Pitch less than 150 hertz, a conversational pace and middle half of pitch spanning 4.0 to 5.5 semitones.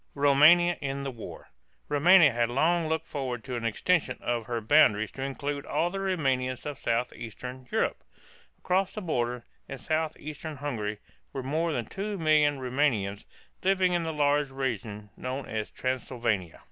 Yes: low, 135 Hz; average, 155 wpm; average, 4.7 semitones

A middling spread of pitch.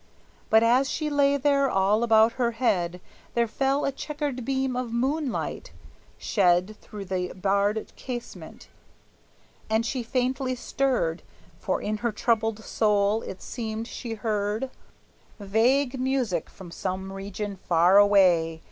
Yes: average, 4.5 semitones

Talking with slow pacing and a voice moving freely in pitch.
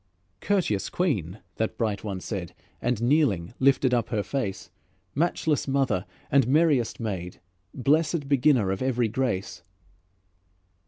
Yes: slow, 120 wpm; wide, 5.8 semitones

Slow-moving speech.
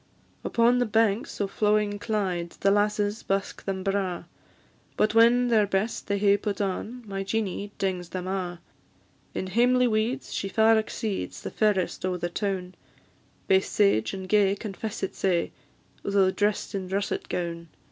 No: average, 155 wpm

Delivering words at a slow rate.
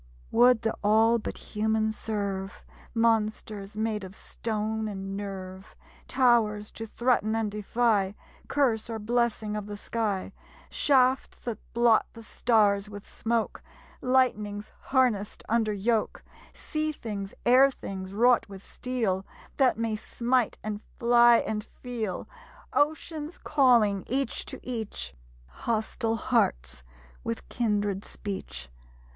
Yes: slow, 120 wpm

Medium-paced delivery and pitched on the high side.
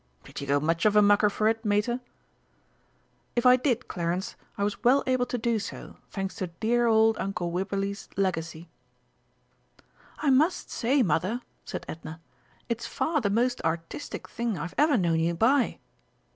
Yes: average, 165 wpm; high, 210 Hz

